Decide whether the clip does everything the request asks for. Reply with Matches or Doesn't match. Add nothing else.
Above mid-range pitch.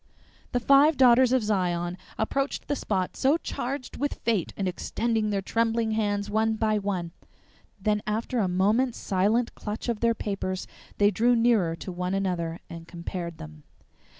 Matches